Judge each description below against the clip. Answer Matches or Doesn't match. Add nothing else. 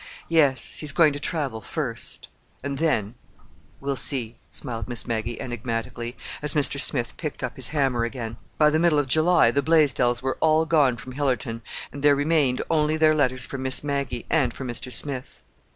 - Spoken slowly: Doesn't match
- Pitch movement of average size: Matches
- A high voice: Doesn't match